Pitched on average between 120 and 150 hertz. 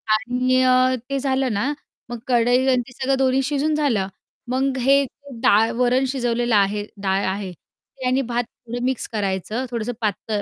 No: high, 245 Hz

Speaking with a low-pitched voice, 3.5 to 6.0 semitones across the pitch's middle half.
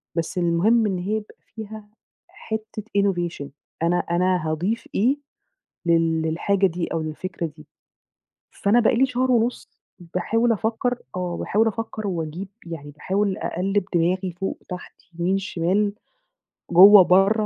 No: high, 190 Hz; average, 4.0 semitones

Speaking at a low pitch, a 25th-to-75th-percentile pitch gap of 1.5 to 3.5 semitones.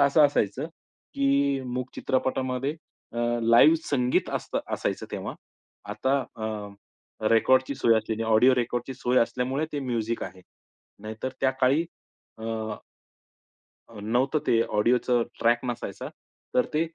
Yes: low, 125 Hz; average, 2.9 semitones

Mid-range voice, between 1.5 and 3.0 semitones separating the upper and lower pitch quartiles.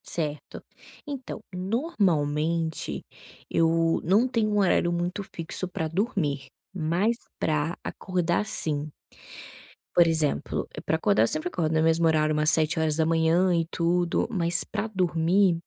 Yes: medium, 165 Hz; average, 2.7 semitones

